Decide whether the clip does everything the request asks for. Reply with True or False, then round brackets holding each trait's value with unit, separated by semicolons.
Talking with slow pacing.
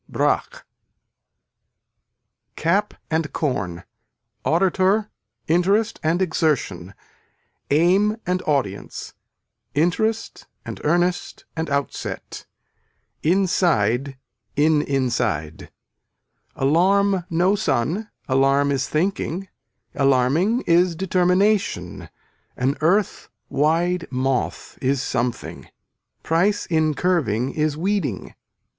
True (80 wpm)